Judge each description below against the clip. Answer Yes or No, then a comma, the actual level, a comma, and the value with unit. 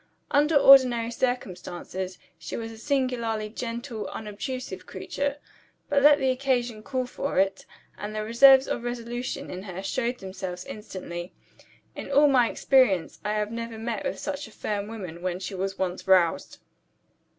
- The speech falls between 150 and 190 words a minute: Yes, average, 155 wpm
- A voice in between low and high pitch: No, high, 230 Hz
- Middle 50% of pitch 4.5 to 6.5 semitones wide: Yes, average, 4.9 semitones